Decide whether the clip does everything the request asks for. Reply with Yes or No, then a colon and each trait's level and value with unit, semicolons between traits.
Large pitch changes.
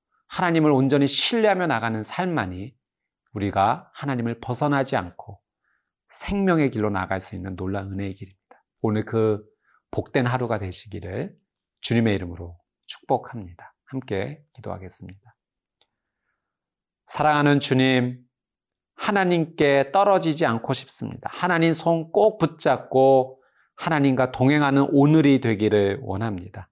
Yes: wide, 6.5 semitones